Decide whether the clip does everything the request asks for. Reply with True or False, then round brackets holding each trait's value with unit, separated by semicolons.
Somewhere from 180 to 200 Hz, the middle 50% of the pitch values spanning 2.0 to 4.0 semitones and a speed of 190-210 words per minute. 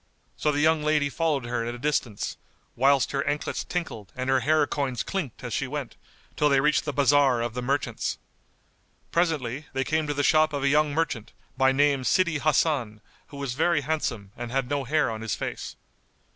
False (140 Hz; 3.2 semitones; 200 wpm)